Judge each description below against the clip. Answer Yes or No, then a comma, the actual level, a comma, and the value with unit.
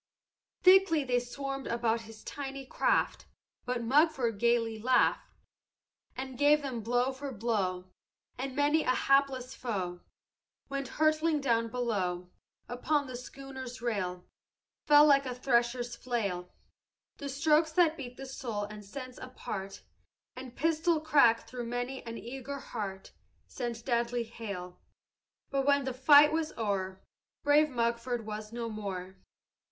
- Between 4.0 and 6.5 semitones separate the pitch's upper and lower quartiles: No, average, 3.5 semitones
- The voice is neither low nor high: No, high, 245 Hz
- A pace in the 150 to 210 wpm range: No, slow, 135 wpm